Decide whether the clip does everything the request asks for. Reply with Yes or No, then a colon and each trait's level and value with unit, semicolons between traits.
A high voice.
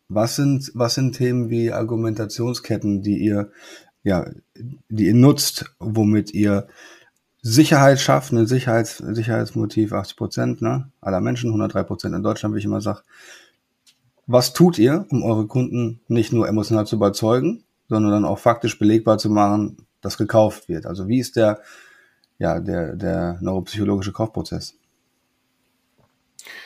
No: low, 110 Hz